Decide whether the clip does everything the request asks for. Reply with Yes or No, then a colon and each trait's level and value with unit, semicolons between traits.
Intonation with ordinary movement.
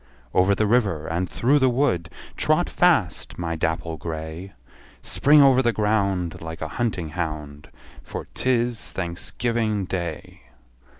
No: wide, 6.2 semitones